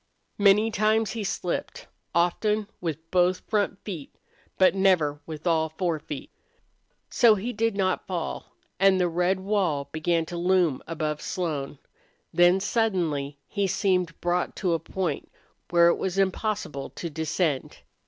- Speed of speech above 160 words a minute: No, average, 145 wpm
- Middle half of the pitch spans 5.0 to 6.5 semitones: No, average, 3.3 semitones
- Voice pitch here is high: No, medium, 180 Hz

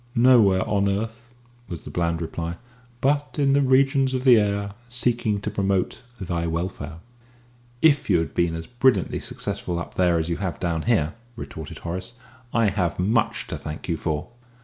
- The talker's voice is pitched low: Yes, low, 100 Hz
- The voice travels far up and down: Yes, wide, 6.0 semitones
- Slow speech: No, average, 170 wpm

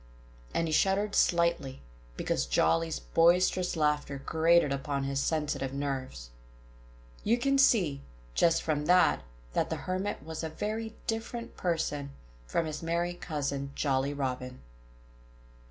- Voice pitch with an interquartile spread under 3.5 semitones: No, average, 4.3 semitones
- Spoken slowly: Yes, slow, 125 wpm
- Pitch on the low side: No, medium, 155 Hz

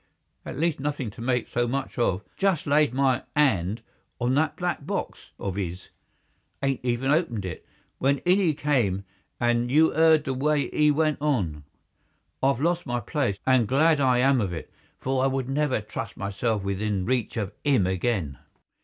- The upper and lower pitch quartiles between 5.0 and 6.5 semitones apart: Yes, wide, 5.6 semitones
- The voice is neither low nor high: No, low, 130 Hz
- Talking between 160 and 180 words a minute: Yes, average, 170 wpm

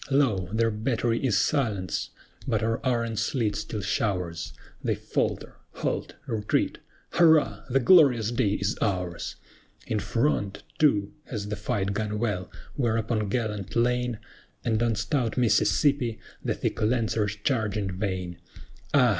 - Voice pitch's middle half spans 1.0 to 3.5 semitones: Yes, average, 3.0 semitones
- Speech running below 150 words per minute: Yes, average, 140 wpm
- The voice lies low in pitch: Yes, low, 110 Hz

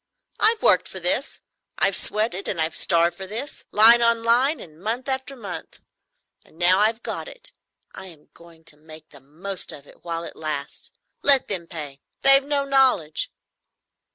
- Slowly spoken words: No, average, 170 wpm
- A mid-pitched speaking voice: No, high, 195 Hz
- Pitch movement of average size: No, wide, 7.7 semitones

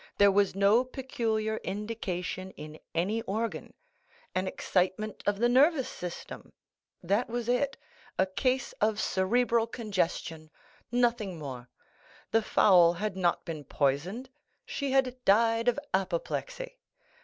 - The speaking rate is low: Yes, slow, 110 wpm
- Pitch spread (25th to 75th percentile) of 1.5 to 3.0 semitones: No, average, 4.7 semitones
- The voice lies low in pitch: No, high, 215 Hz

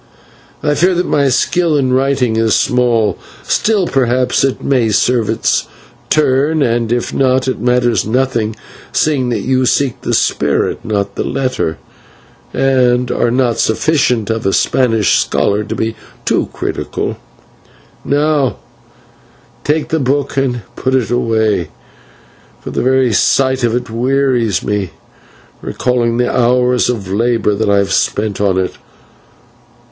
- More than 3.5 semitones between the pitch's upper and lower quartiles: No, average, 3.0 semitones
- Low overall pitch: Yes, low, 125 Hz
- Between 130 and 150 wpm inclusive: Yes, average, 140 wpm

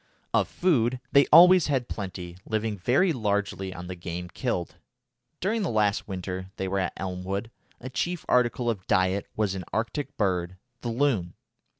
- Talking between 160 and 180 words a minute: Yes, average, 165 wpm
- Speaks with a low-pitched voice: Yes, low, 105 Hz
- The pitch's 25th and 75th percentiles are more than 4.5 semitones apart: Yes, wide, 5.4 semitones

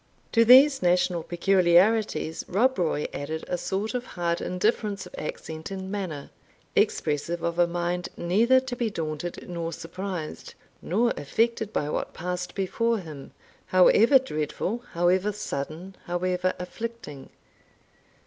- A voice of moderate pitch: Yes, medium, 180 Hz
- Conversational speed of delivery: No, slow, 130 wpm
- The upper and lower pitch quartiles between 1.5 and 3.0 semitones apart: No, average, 4.2 semitones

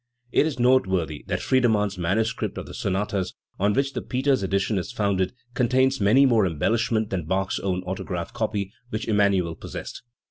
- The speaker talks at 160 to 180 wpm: Yes, average, 165 wpm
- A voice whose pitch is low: Yes, low, 105 Hz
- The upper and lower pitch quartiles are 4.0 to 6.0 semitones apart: Yes, average, 4.3 semitones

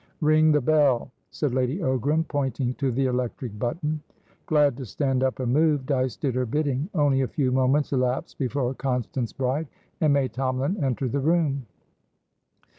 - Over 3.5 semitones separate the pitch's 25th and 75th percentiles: No, average, 2.7 semitones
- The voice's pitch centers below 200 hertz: Yes, low, 135 Hz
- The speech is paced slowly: No, average, 165 wpm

